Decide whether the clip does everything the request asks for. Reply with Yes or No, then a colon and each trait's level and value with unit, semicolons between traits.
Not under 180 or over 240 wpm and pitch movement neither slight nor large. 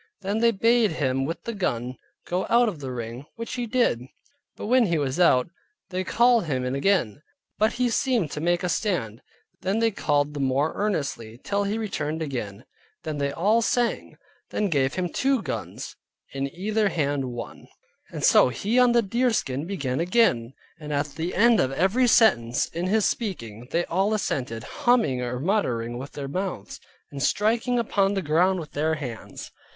No: average, 185 wpm; wide, 8.1 semitones